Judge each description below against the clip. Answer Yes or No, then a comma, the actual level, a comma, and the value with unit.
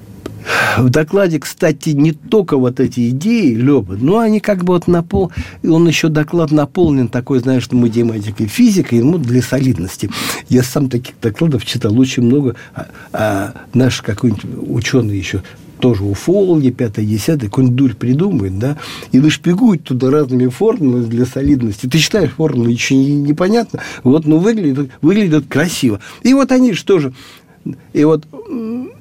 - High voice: No, low, 135 Hz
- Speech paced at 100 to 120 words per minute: No, average, 155 wpm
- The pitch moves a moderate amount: Yes, average, 4.8 semitones